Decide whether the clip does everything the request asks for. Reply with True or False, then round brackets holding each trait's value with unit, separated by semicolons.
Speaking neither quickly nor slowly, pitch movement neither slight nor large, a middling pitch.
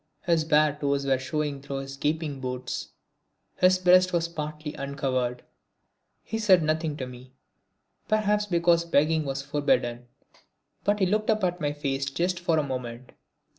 True (155 wpm; 4.2 semitones; 150 Hz)